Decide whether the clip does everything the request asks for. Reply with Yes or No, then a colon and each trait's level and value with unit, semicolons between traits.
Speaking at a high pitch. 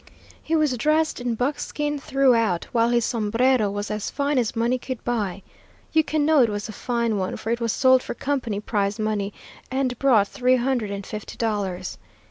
Yes: high, 235 Hz